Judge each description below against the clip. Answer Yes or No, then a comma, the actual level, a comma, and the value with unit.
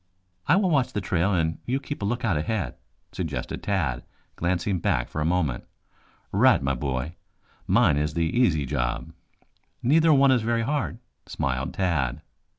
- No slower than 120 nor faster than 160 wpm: Yes, average, 155 wpm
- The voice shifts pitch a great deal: Yes, wide, 8.1 semitones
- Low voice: Yes, very low, 90 Hz